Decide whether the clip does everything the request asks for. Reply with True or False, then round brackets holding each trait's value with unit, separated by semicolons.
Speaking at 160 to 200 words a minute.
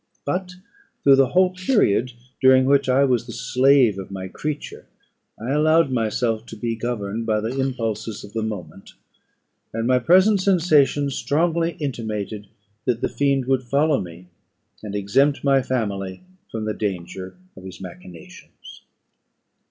False (145 wpm)